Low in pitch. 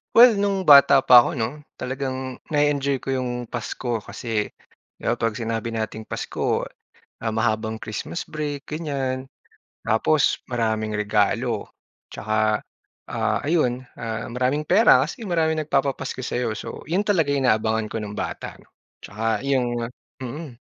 Yes: low, 130 Hz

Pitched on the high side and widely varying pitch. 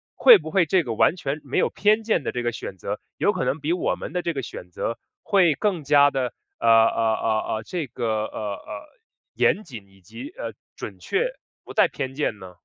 No: low, 135 Hz; wide, 7.2 semitones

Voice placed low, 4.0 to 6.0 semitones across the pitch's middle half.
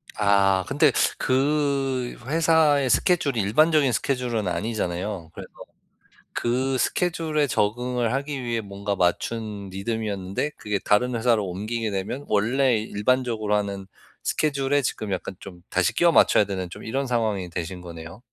Yes: low, 115 Hz; average, 5.2 semitones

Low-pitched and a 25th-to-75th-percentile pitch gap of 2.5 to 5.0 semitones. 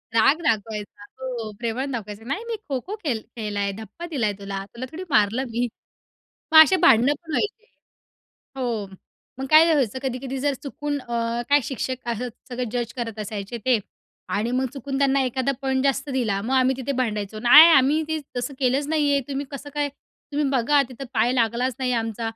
No: very high, 255 Hz; average, 3.7 semitones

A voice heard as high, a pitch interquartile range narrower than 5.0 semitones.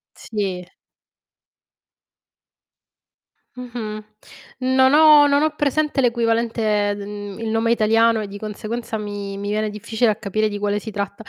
Yes: high, 220 Hz; narrow, 2.6 semitones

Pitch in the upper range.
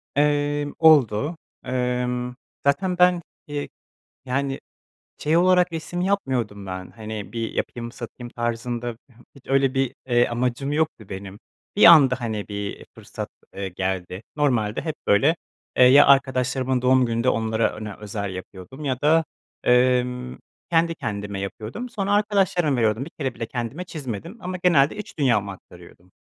No: low, 125 Hz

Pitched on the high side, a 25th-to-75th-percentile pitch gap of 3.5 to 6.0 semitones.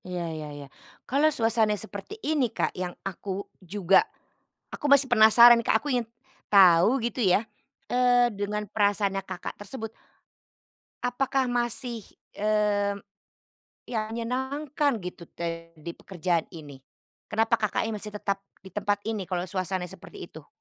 Yes: high, 210 Hz; average, 4.3 semitones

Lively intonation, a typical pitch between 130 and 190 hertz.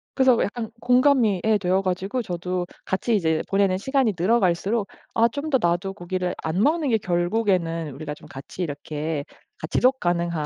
No: average, 4.9 semitones; medium, 185 Hz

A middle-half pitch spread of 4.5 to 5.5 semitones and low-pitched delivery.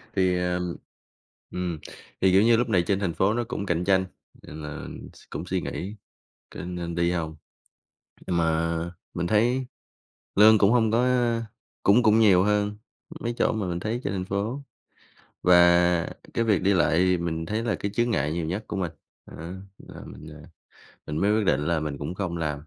No: average, 3.7 semitones; very low, 90 Hz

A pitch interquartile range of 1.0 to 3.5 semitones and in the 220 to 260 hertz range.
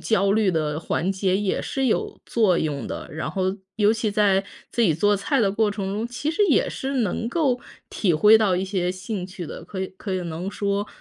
No: average, 3.1 semitones; high, 200 Hz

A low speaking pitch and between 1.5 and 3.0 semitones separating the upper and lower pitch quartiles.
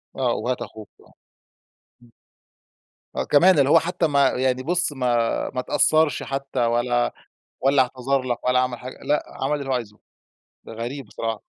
Yes: low, 130 Hz; narrow, 2.6 semitones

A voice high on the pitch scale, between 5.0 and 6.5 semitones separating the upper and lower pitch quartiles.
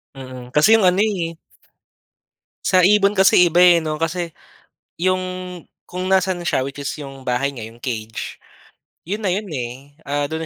No: medium, 165 Hz; average, 5.3 semitones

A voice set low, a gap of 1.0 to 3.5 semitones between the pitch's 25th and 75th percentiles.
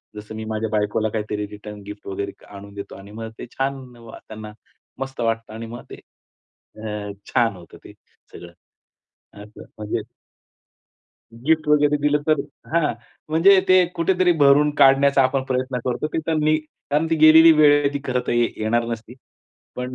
No: low, 125 Hz; wide, 5.5 semitones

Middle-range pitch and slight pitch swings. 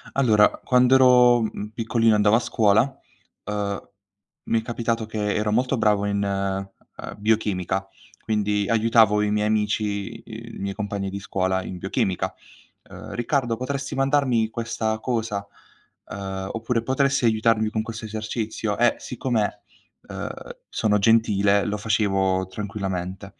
No: low, 110 Hz; narrow, 2.3 semitones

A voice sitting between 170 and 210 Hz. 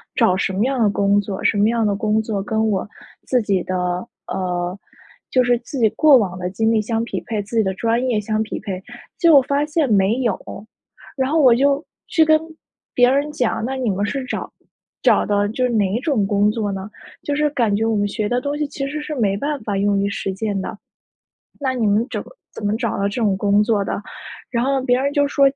No: high, 220 Hz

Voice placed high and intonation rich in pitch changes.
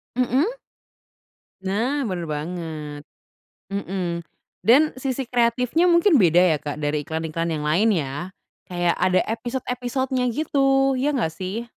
Yes: high, 200 Hz; wide, 7.6 semitones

